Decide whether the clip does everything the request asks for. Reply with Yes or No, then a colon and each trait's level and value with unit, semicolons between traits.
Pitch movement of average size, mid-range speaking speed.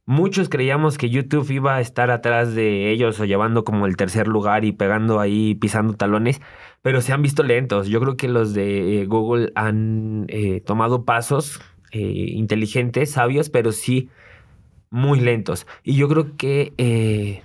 Yes: average, 3.6 semitones; average, 165 wpm